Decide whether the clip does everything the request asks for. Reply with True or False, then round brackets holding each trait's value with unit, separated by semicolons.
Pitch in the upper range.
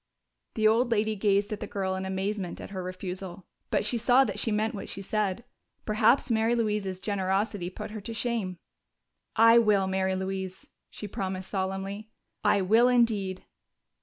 True (200 Hz)